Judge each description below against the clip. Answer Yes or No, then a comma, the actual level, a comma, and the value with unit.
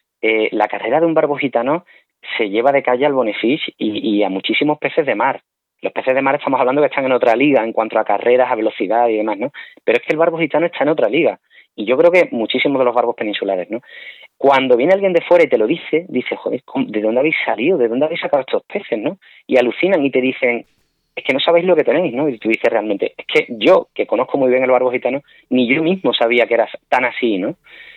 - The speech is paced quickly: Yes, fast, 255 wpm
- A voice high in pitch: No, medium, 140 Hz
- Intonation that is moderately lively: No, wide, 6.0 semitones